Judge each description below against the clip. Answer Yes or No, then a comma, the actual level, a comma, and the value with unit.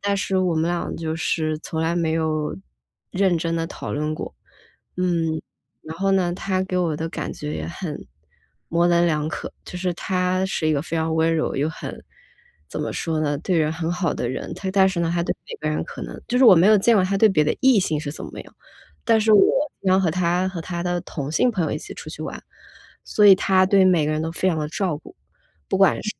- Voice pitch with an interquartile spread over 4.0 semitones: No, average, 2.9 semitones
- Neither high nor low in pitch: Yes, medium, 170 Hz